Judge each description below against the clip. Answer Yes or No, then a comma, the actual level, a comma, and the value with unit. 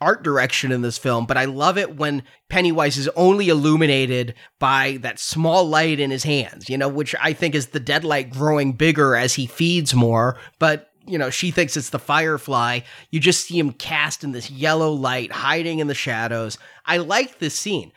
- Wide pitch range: No, average, 3.5 semitones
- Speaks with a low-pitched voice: No, medium, 145 Hz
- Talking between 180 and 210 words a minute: Yes, average, 200 wpm